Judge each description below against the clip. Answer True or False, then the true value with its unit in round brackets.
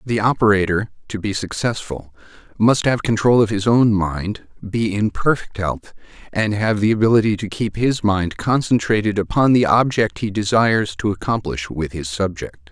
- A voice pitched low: True (105 Hz)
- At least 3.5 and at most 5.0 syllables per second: True (4.8 syllables/s)